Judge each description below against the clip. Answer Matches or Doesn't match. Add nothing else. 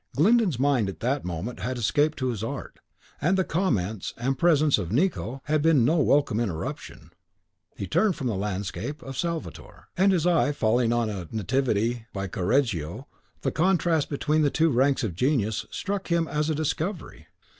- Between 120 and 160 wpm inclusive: Doesn't match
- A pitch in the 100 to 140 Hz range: Matches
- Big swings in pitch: Matches